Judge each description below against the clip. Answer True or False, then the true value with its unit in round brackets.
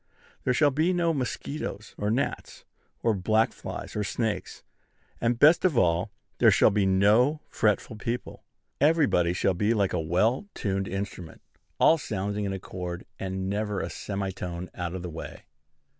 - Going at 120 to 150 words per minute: False (160 wpm)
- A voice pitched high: False (105 Hz)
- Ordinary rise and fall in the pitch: True (4.7 semitones)